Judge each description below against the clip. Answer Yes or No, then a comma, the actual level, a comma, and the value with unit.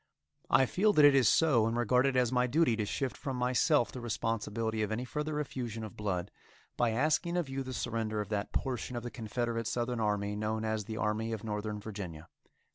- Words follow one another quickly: Yes, fast, 210 wpm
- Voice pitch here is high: No, low, 115 Hz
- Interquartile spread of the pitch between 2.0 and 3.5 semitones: Yes, average, 3.2 semitones